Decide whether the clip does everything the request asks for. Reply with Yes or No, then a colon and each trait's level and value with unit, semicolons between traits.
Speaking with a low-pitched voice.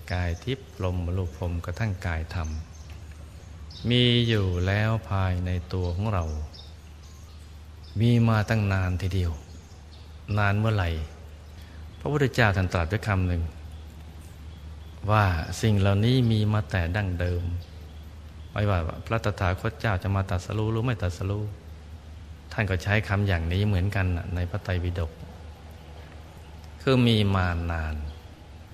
Yes: very low, 90 Hz